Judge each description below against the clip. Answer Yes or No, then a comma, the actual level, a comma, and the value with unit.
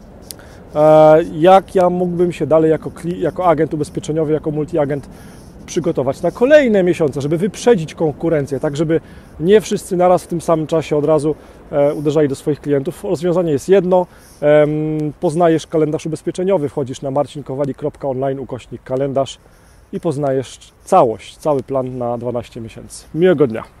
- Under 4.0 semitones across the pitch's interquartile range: Yes, average, 3.2 semitones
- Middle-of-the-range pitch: Yes, medium, 155 Hz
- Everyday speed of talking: Yes, average, 130 wpm